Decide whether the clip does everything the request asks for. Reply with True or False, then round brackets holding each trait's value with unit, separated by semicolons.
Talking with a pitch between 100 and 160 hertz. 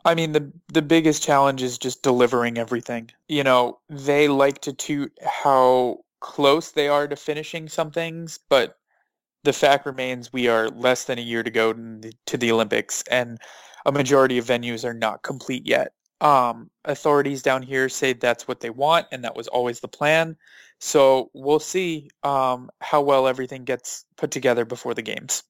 True (135 Hz)